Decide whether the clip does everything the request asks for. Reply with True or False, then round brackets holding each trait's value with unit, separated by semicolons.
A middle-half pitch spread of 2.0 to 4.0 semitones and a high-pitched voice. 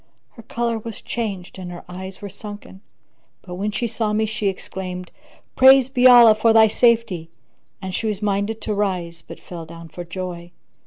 True (3.7 semitones; 205 Hz)